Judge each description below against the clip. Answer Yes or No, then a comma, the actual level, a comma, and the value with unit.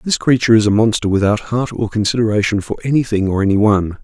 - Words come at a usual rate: Yes, average, 195 wpm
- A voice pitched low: Yes, low, 110 Hz